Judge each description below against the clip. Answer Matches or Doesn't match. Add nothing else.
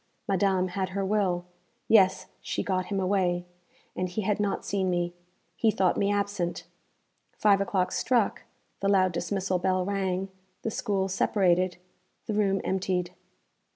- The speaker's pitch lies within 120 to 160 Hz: Doesn't match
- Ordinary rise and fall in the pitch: Doesn't match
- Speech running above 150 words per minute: Doesn't match